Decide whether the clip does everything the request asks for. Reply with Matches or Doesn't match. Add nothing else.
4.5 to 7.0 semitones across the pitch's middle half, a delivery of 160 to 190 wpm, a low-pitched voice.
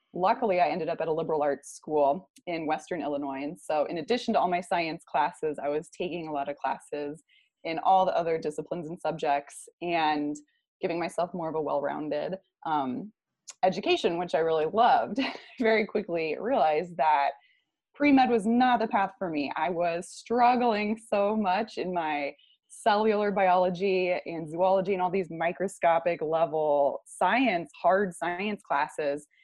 Doesn't match